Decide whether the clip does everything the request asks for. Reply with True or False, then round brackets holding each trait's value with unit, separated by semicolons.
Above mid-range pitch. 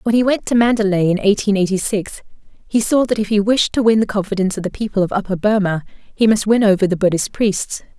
True (205 Hz)